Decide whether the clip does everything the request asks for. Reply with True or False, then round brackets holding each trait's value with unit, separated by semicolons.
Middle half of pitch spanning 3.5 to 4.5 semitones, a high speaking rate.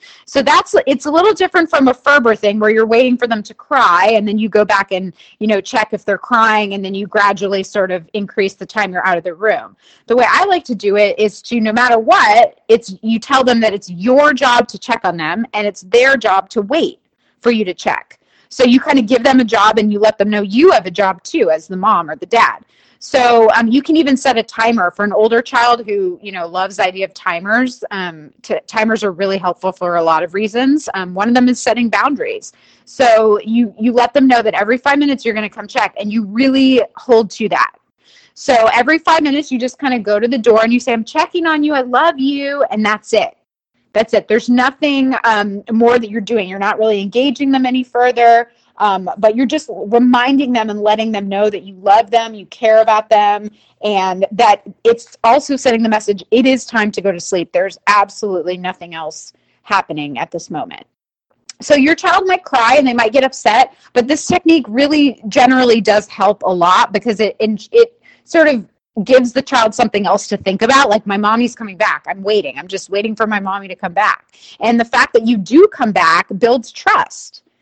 True (4.1 semitones; 230 wpm)